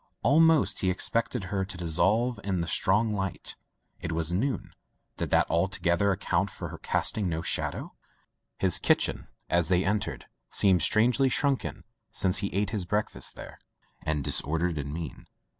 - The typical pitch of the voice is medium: No, very low, 95 Hz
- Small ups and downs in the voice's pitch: No, average, 3.8 semitones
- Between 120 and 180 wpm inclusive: Yes, average, 160 wpm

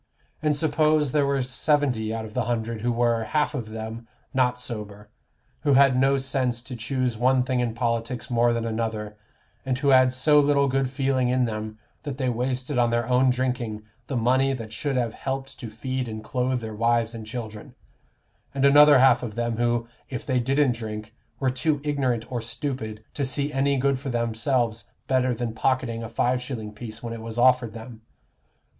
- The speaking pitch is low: Yes, low, 125 Hz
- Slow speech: No, average, 190 wpm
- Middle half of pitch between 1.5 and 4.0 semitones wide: Yes, narrow, 2.6 semitones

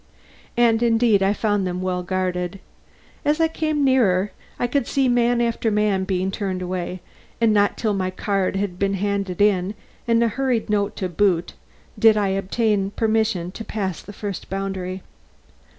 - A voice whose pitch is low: No, high, 200 Hz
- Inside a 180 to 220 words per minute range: No, average, 165 wpm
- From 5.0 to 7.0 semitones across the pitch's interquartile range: No, average, 3.3 semitones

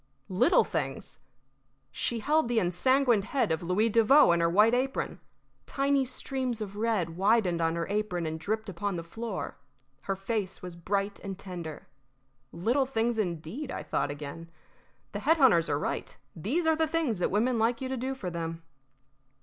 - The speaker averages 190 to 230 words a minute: No, average, 175 wpm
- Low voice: No, high, 205 Hz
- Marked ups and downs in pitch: Yes, wide, 6.4 semitones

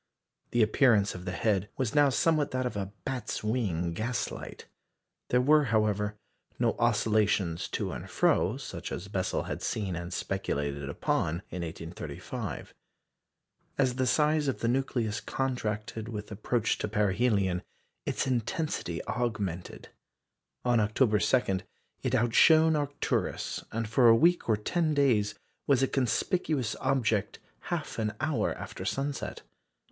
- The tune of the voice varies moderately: Yes, average, 4.4 semitones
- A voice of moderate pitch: No, low, 110 Hz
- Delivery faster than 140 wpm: No, slow, 135 wpm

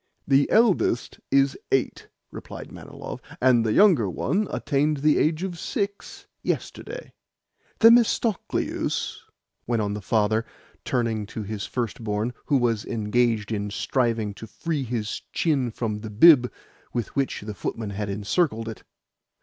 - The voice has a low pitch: Yes, low, 120 Hz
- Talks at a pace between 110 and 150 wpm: Yes, average, 140 wpm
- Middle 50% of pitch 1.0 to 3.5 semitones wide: No, wide, 5.6 semitones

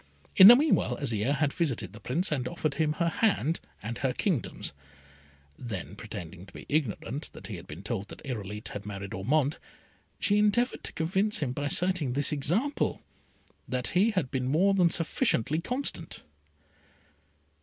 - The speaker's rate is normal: Yes, average, 165 wpm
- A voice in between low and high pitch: Yes, medium, 145 Hz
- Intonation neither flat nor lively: No, wide, 7.5 semitones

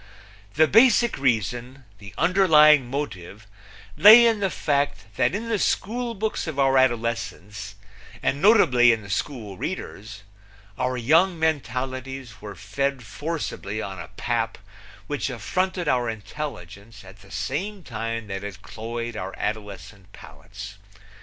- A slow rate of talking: Yes, slow, 130 wpm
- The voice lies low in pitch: Yes, low, 125 Hz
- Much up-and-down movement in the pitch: Yes, wide, 6.7 semitones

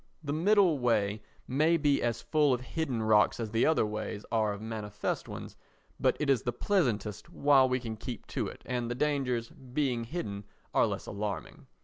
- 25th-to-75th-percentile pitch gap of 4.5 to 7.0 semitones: Yes, average, 4.9 semitones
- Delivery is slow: No, average, 190 wpm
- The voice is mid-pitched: No, low, 120 Hz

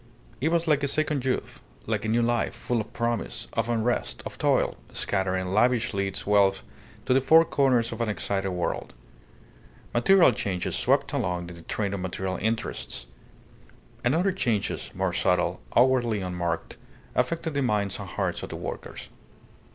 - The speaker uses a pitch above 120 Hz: No, low, 115 Hz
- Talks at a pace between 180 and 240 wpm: No, average, 165 wpm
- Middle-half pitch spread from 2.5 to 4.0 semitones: No, average, 4.9 semitones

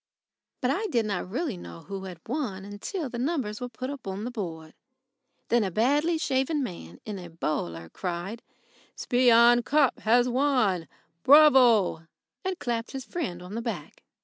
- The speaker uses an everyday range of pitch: No, wide, 6.0 semitones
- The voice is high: Yes, high, 235 Hz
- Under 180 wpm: Yes, average, 165 wpm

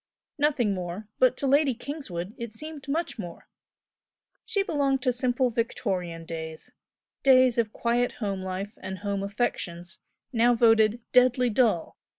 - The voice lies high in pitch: Yes, high, 235 Hz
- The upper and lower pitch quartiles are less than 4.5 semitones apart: No, average, 5.0 semitones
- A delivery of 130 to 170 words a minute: Yes, average, 140 wpm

